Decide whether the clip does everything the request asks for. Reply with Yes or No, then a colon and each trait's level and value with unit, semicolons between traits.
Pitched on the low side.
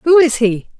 No: very high, 265 Hz